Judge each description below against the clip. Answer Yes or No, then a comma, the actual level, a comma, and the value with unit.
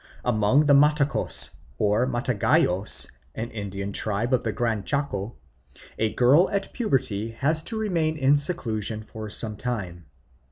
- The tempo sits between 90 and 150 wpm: Yes, slow, 135 wpm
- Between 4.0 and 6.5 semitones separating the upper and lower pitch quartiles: Yes, average, 5.2 semitones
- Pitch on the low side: Yes, low, 120 Hz